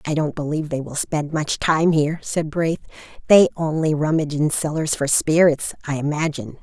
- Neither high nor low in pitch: Yes, medium, 155 Hz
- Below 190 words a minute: Yes, average, 180 wpm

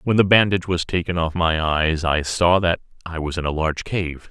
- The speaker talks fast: Yes, fast, 235 wpm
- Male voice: Yes, male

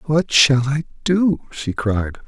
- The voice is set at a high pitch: No, medium, 145 Hz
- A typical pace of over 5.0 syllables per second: No, 3.4 syllables/s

